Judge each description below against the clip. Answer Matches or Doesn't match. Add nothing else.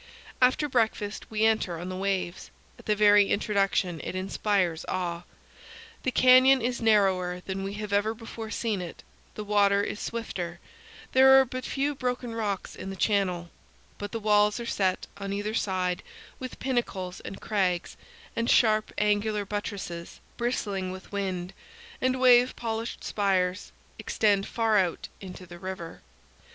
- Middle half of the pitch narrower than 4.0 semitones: Matches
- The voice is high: Matches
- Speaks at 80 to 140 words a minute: Doesn't match